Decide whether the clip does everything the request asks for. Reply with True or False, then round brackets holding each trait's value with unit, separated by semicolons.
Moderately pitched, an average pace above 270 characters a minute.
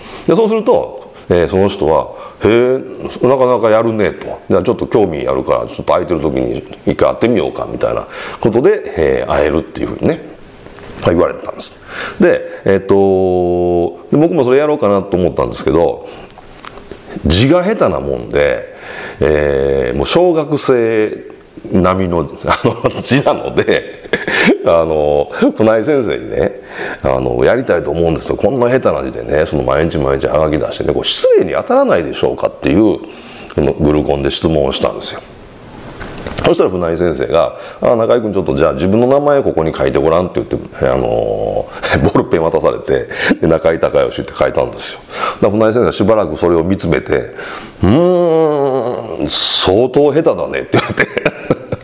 True (145 Hz; 345 characters per minute)